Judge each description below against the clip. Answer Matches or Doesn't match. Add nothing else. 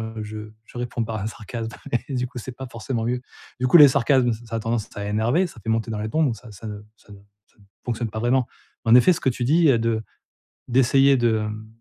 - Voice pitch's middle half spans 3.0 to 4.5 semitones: Doesn't match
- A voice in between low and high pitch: Doesn't match